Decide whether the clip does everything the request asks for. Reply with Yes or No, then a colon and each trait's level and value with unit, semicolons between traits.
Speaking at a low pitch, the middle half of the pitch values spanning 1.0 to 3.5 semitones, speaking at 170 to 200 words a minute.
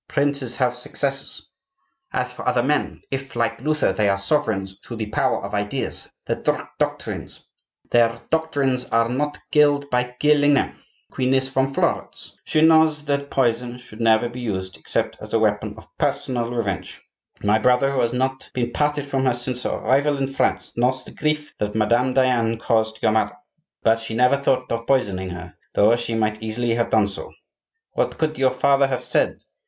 Yes: low, 125 Hz; average, 3.2 semitones; average, 180 wpm